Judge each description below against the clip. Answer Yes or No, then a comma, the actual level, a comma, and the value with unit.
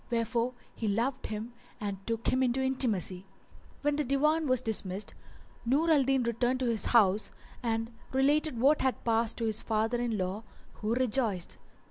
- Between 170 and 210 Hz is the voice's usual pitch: No, high, 235 Hz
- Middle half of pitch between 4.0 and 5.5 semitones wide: No, average, 3.3 semitones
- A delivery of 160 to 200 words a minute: Yes, average, 165 wpm